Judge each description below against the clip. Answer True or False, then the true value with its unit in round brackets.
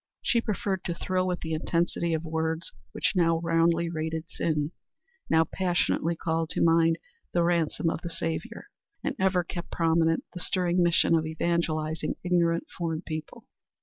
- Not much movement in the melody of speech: True (1.3 semitones)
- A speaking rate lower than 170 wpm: True (155 wpm)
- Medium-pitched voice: True (165 Hz)